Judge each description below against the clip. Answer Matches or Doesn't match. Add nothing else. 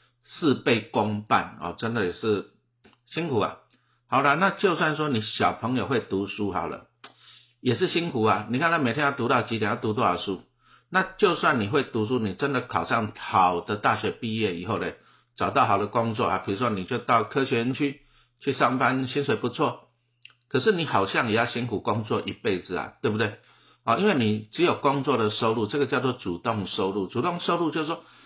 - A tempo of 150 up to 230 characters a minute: Doesn't match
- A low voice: Matches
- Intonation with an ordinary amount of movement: Matches